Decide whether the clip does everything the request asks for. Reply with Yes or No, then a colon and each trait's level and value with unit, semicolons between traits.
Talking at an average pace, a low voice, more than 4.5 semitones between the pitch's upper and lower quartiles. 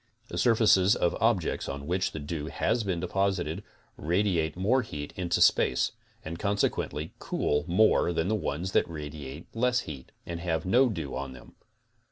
Yes: average, 165 wpm; very low, 85 Hz; average, 4.9 semitones